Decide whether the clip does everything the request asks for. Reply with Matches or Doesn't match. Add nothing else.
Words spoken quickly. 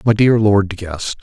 Matches